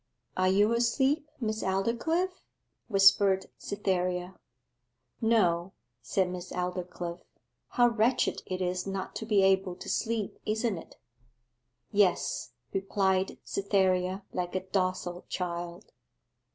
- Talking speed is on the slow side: Yes, slow, 110 wpm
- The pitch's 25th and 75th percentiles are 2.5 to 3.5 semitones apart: Yes, average, 3.0 semitones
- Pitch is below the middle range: No, high, 190 Hz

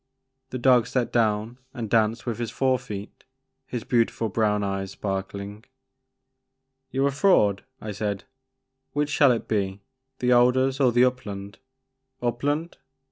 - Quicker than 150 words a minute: No, average, 145 wpm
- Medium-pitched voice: No, low, 120 Hz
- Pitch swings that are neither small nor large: Yes, average, 3.8 semitones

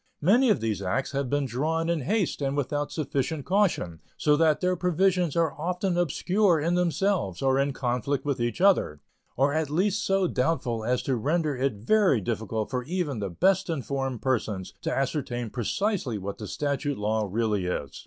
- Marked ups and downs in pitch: Yes, wide, 6.4 semitones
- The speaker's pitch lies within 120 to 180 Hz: Yes, medium, 140 Hz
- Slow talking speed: No, average, 180 wpm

